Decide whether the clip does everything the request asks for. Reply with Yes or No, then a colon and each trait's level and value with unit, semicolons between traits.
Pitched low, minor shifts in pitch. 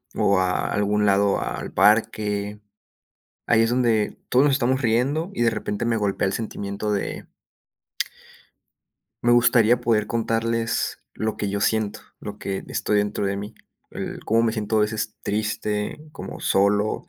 Yes: low, 110 Hz; narrow, 2.0 semitones